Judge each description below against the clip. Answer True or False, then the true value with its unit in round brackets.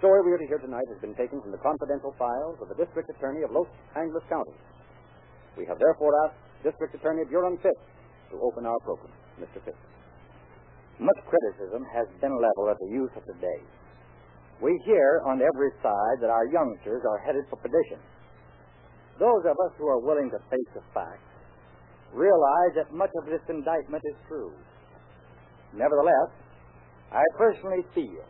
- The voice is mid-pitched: True (150 Hz)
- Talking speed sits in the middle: True (170 wpm)